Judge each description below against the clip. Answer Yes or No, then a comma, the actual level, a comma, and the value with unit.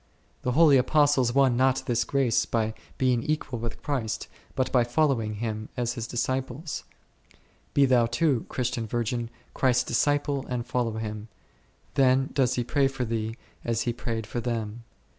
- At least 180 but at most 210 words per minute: No, average, 160 wpm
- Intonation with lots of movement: No, narrow, 2.6 semitones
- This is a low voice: Yes, low, 125 Hz